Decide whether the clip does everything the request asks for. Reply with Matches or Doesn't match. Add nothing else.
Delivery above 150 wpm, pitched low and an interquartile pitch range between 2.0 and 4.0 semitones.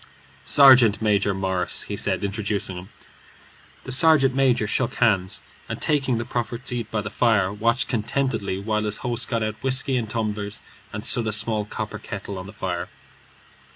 Matches